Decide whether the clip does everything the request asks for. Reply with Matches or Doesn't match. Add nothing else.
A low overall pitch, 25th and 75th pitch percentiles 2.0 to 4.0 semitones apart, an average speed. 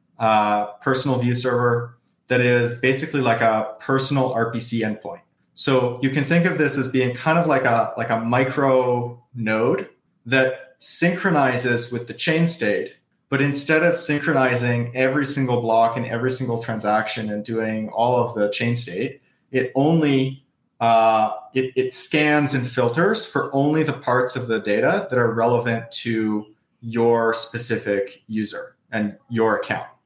Matches